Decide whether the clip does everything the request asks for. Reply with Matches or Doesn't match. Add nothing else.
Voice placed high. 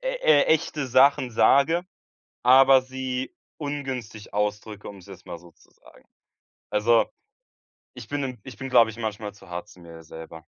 Doesn't match